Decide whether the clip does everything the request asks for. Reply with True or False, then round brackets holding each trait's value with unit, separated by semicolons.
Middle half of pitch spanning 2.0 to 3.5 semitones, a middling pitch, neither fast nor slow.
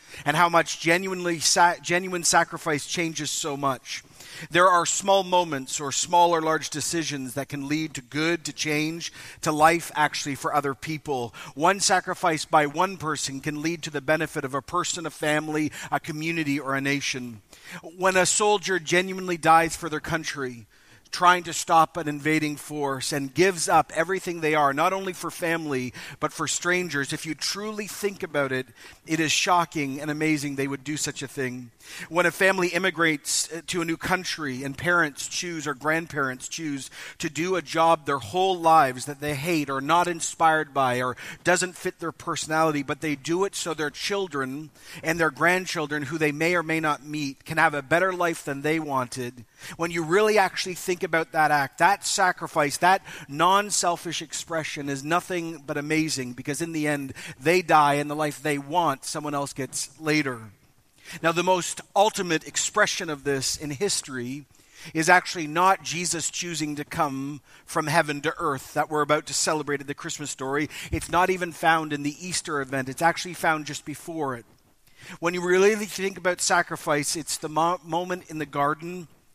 True (3.1 semitones; 160 Hz; 185 wpm)